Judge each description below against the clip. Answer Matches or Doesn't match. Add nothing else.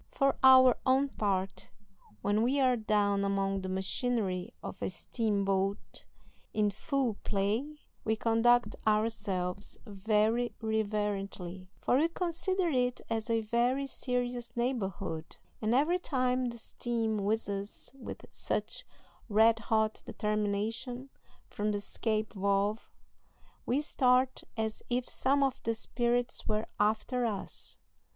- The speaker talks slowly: Matches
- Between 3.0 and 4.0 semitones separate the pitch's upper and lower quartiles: Matches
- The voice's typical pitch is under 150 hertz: Doesn't match